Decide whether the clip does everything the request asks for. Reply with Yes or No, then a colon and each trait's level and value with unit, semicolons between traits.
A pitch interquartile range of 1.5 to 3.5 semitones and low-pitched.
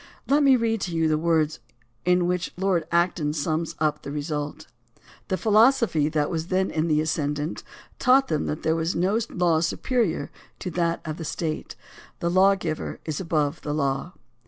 No: average, 3.2 semitones; medium, 165 Hz